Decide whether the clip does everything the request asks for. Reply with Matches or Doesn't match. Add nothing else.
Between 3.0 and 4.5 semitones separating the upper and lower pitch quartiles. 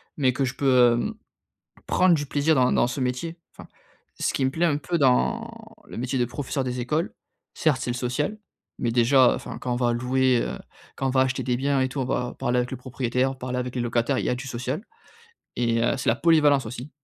Doesn't match